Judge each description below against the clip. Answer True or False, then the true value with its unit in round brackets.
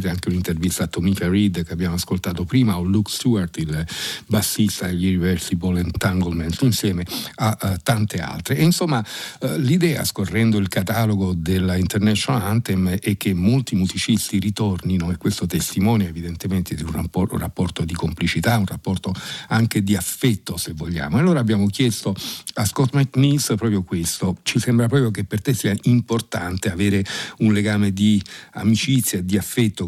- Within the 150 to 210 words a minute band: True (155 wpm)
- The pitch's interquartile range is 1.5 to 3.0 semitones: False (3.9 semitones)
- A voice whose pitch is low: True (100 Hz)